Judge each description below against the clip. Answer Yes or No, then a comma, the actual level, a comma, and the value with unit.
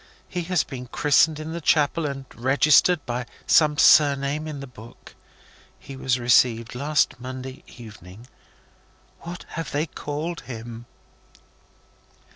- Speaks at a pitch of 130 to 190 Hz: Yes, medium, 140 Hz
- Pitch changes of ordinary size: Yes, average, 3.8 semitones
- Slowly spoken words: Yes, slow, 125 wpm